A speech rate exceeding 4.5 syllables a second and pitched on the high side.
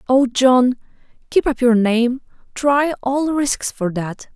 No: 3.3 syllables/s; very high, 255 Hz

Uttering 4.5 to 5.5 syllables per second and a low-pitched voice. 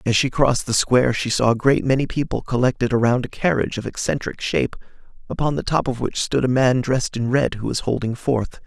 No: 6.0 syllables/s; low, 125 Hz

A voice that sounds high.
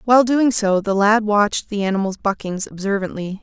Yes: high, 205 Hz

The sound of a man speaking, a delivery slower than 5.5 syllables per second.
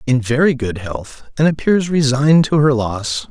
Yes: male; 4.5 syllables/s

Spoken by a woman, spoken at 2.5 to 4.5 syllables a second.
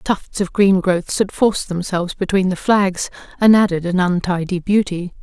No: female; 4.8 syllables/s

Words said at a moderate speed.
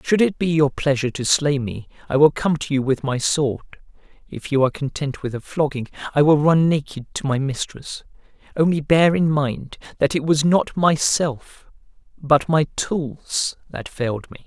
Yes: average, 185 wpm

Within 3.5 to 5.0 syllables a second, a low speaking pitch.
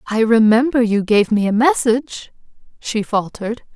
No: 4.8 syllables/s; high, 230 Hz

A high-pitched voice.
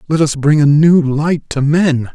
No: medium, 150 Hz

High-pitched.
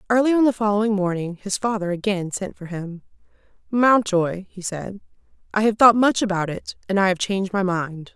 Yes: high, 200 Hz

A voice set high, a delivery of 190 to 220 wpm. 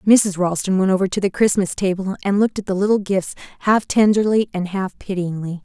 Yes: high, 195 Hz; average, 200 wpm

